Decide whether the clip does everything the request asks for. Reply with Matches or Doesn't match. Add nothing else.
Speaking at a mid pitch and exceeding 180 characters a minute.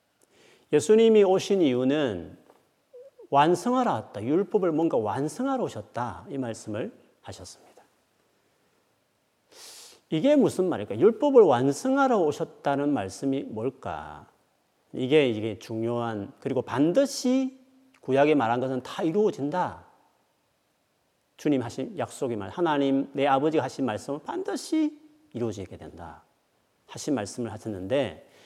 Matches